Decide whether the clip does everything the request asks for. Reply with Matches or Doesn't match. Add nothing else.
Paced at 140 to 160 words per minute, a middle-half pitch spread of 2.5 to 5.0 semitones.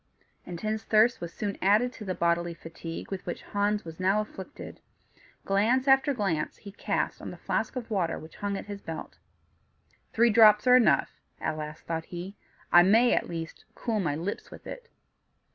Doesn't match